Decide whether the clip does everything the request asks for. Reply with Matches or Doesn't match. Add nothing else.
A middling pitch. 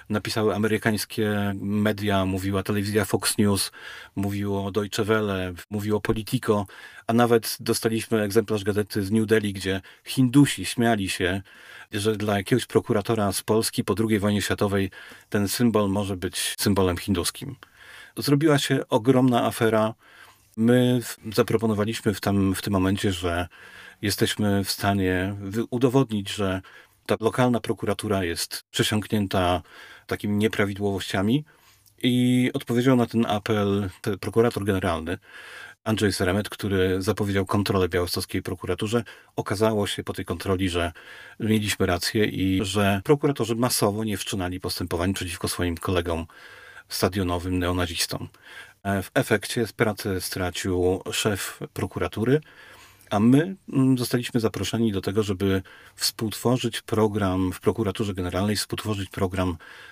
Doesn't match